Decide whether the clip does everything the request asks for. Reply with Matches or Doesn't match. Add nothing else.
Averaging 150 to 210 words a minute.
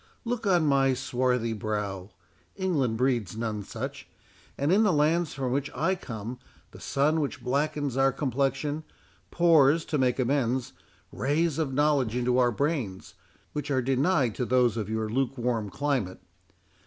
Doesn't match